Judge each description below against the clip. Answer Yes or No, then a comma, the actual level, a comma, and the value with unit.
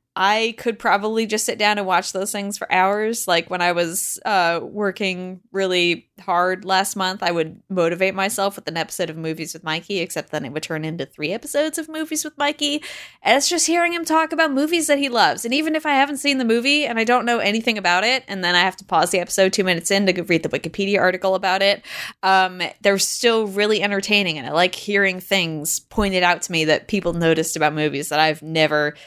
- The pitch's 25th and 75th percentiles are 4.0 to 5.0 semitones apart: Yes, average, 4.6 semitones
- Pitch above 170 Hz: Yes, high, 190 Hz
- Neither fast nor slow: No, fast, 230 wpm